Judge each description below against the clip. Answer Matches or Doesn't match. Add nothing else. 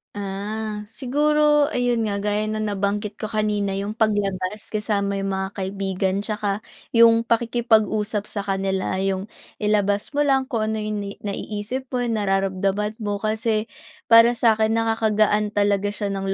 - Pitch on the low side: Doesn't match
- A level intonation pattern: Matches